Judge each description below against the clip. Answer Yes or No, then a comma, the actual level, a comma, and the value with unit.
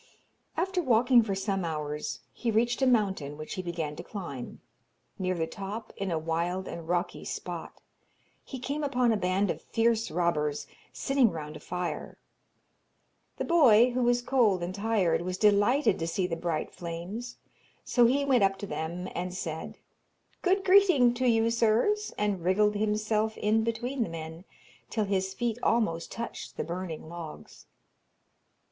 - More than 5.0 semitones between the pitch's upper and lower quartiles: Yes, wide, 5.6 semitones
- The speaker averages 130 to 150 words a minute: No, average, 160 wpm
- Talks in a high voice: Yes, high, 205 Hz